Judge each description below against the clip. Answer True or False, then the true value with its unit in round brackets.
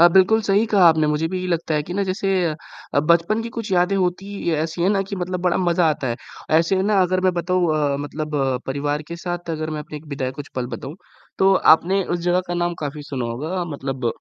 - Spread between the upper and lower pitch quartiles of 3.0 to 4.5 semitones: True (3.6 semitones)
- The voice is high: False (170 Hz)